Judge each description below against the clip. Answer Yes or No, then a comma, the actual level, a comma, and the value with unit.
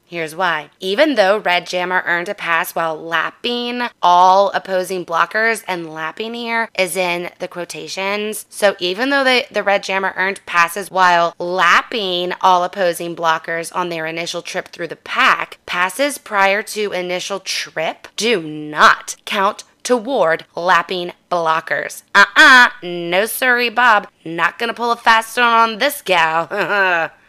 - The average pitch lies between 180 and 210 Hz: Yes, medium, 185 Hz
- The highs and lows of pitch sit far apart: No, average, 3.8 semitones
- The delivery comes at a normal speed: Yes, average, 150 wpm